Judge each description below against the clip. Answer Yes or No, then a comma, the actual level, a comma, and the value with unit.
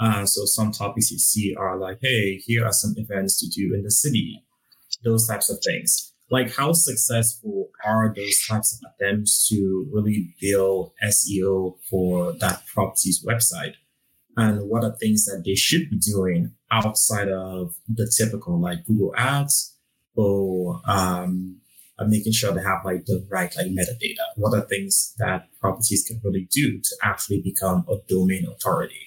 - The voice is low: Yes, low, 105 Hz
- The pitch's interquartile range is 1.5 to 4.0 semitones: Yes, average, 3.2 semitones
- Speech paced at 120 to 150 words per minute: No, average, 165 wpm